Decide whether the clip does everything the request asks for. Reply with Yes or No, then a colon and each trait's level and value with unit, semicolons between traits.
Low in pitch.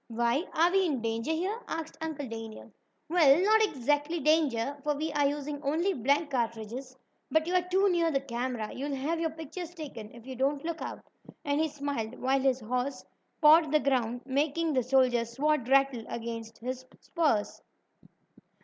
No: very high, 280 Hz